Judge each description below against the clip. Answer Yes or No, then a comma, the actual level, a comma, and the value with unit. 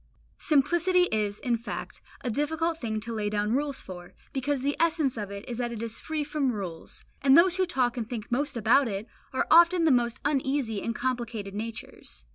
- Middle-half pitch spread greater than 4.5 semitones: Yes, average, 5.1 semitones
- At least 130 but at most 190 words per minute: No, average, 200 wpm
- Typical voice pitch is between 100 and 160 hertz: No, high, 245 Hz